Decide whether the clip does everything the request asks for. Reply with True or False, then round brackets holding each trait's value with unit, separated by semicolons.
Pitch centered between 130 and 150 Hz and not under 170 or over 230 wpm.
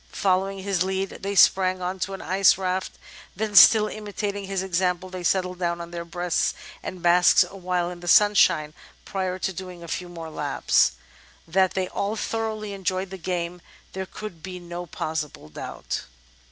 False (185 Hz; 175 wpm)